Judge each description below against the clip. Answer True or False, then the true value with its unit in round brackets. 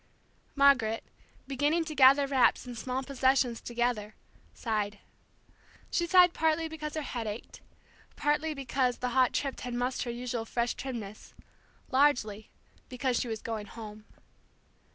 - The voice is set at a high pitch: True (250 Hz)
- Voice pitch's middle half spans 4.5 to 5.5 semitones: False (3.4 semitones)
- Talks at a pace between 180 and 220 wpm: False (135 wpm)